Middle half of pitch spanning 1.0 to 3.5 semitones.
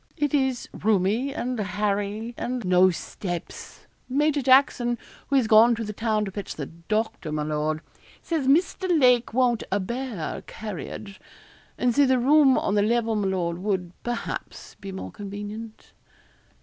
No: average, 4.4 semitones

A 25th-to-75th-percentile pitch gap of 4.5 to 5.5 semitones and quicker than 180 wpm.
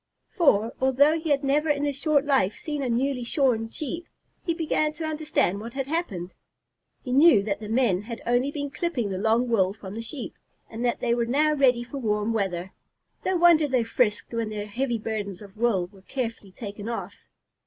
Yes: average, 5.1 semitones; average, 200 wpm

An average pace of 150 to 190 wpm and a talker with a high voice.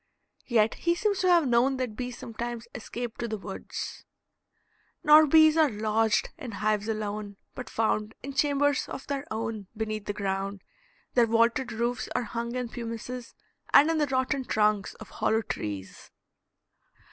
Yes: average, 160 wpm; high, 235 Hz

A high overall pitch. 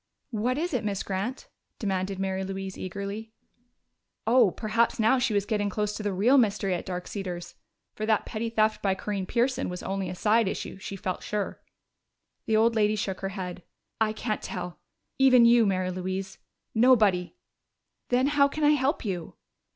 Yes: high, 210 Hz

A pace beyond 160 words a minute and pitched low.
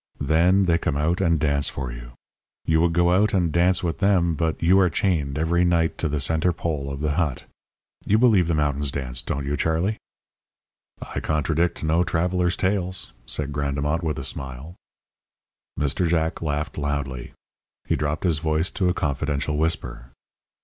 Yes: average, 170 wpm; very low, 80 Hz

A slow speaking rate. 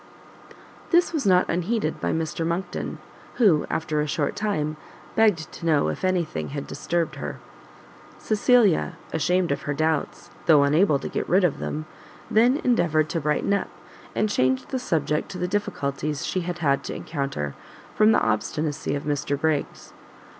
No: average, 165 wpm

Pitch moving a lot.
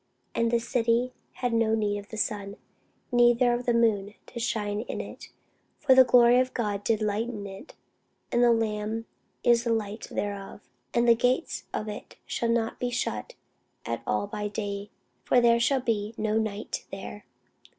No: narrow, 2.6 semitones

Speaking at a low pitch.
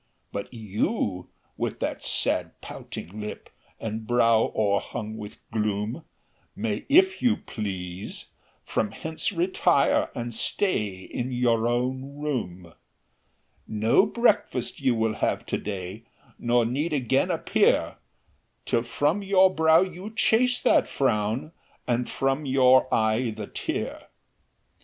Yes: low, 120 Hz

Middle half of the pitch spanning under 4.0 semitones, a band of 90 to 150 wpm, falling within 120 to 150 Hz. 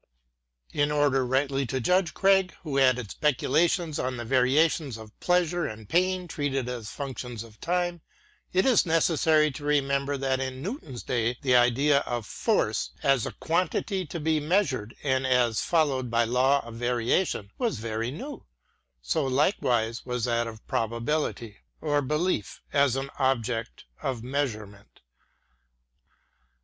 No: average, 4.5 semitones; average, 140 wpm; low, 135 Hz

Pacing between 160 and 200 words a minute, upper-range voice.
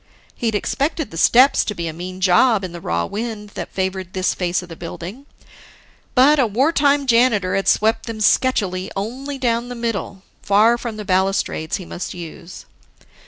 Yes: average, 175 wpm; high, 210 Hz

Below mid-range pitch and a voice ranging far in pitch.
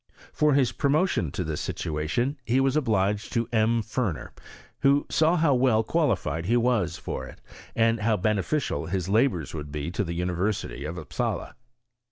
Yes: low, 110 Hz; wide, 6.9 semitones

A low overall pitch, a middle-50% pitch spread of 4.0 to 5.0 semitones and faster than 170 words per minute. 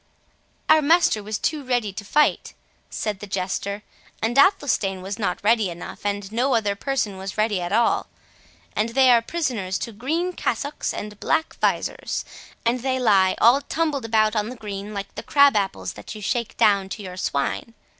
No: high, 215 Hz; average, 4.4 semitones; average, 180 wpm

